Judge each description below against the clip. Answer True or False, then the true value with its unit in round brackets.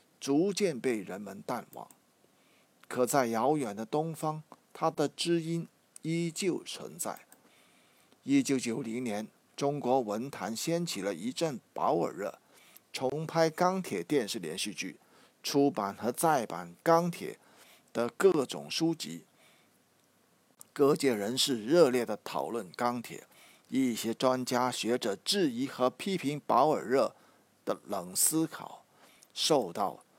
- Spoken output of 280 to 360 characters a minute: False (180 characters per minute)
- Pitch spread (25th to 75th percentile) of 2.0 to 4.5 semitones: False (5.4 semitones)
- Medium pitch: True (145 Hz)